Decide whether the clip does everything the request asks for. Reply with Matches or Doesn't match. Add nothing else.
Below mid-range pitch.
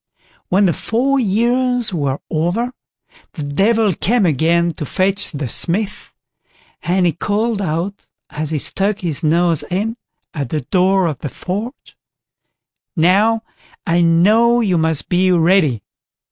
Doesn't match